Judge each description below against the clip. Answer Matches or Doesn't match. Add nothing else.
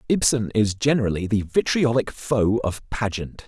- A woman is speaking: Doesn't match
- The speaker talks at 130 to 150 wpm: Matches